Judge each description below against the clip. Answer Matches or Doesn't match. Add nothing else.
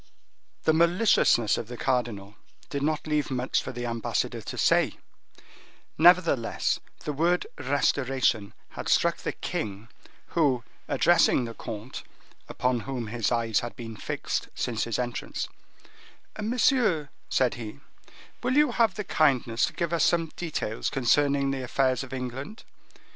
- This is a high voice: Doesn't match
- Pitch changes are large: Matches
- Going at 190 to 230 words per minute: Doesn't match